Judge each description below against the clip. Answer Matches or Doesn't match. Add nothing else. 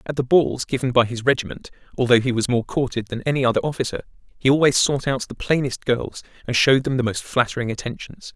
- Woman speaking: Doesn't match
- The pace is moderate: Doesn't match